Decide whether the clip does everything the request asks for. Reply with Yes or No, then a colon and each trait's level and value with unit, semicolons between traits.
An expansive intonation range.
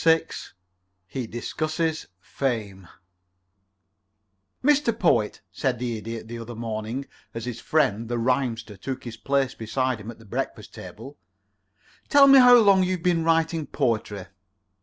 Yes: wide, 6.3 semitones